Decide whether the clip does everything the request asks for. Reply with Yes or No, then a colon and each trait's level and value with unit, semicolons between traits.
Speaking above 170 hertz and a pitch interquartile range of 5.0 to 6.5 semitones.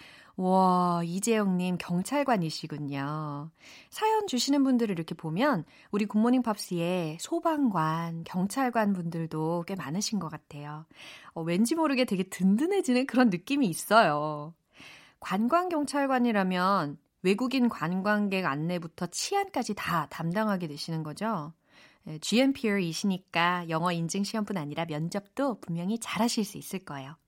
Yes: medium, 185 Hz; wide, 5.6 semitones